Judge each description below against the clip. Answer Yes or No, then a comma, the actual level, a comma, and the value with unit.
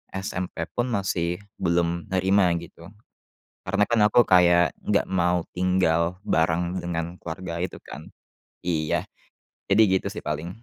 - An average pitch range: No, narrow, 1.9 semitones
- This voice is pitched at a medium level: No, very low, 90 Hz